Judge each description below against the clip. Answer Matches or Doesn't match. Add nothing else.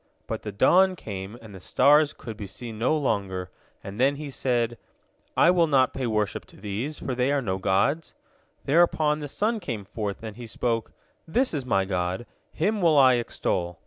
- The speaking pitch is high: Doesn't match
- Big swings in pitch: Matches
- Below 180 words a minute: Doesn't match